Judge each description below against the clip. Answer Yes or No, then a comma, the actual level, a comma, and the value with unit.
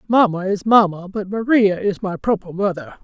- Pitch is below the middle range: No, high, 195 Hz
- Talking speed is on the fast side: No, average, 180 wpm